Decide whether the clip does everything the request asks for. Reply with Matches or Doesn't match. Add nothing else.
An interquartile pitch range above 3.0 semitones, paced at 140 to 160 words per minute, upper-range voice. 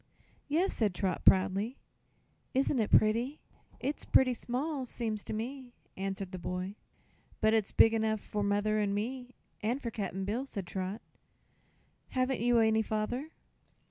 Matches